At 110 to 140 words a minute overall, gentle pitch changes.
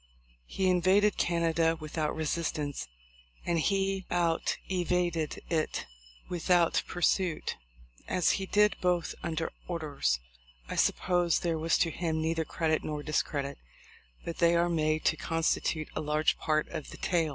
Yes: slow, 135 wpm; narrow, 2.1 semitones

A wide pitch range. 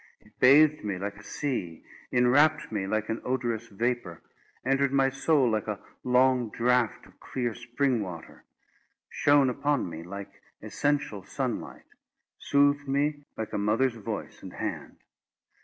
No: average, 4.7 semitones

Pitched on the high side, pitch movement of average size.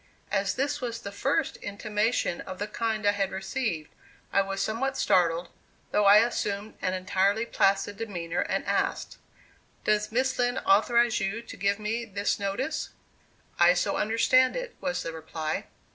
Yes: high, 205 Hz; average, 3.2 semitones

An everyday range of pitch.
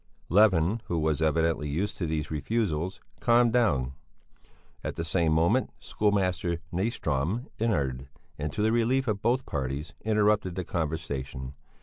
No: wide, 5.9 semitones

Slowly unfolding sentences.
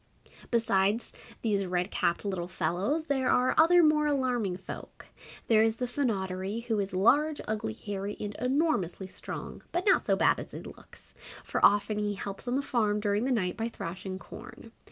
No: average, 175 wpm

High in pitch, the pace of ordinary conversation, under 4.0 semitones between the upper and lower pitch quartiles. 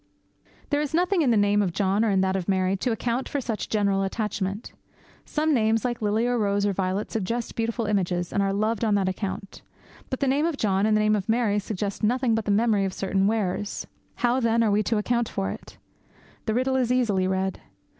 No: high, 215 Hz; fast, 225 wpm; average, 3.3 semitones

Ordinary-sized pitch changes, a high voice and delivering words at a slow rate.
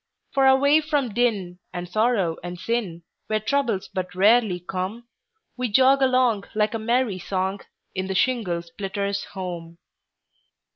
Yes: average, 4.9 semitones; high, 210 Hz; slow, 125 wpm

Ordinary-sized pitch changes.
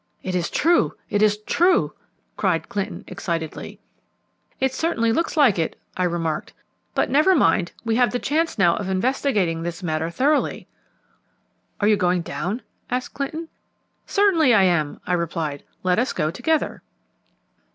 No: wide, 7.9 semitones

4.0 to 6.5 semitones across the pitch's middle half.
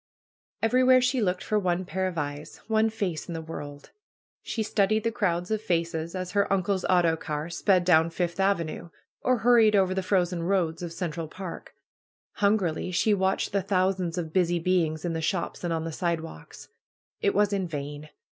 No: average, 3.3 semitones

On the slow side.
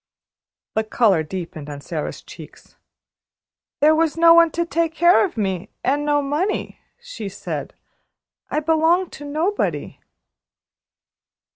Yes: slow, 125 wpm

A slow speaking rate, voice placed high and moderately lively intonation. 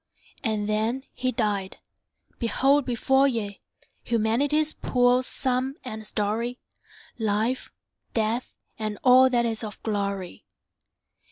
Yes: slow, 105 wpm; high, 230 Hz; average, 3.2 semitones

